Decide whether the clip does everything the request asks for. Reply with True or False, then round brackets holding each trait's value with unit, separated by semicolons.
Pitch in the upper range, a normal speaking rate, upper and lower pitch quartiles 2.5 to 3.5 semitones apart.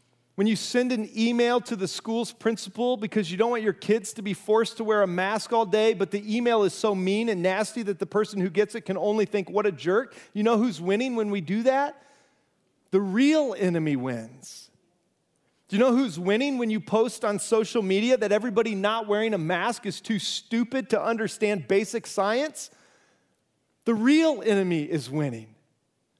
True (215 Hz; 195 wpm; 3.0 semitones)